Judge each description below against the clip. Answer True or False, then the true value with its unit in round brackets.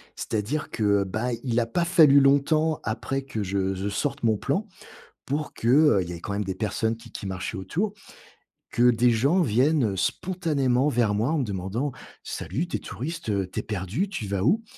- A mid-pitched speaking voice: False (120 Hz)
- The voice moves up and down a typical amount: False (6.5 semitones)